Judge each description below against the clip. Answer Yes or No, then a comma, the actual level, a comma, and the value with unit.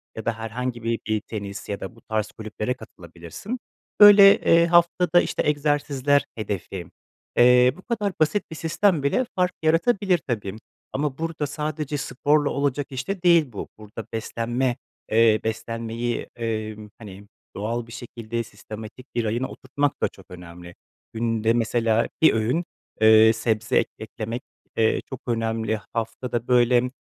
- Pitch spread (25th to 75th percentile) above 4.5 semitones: Yes, average, 4.9 semitones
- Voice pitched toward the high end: No, low, 120 Hz